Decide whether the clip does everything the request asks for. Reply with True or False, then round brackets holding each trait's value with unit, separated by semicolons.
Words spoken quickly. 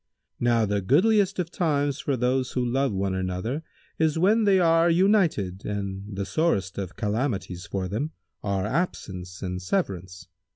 False (155 wpm)